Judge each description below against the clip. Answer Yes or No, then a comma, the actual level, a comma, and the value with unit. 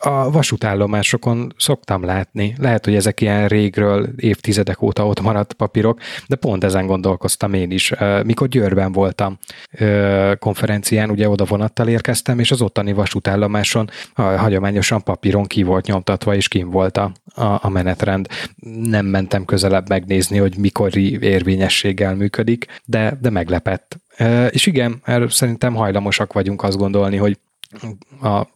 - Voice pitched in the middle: No, low, 100 Hz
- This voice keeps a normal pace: Yes, average, 130 wpm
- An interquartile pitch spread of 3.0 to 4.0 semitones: No, narrow, 2.5 semitones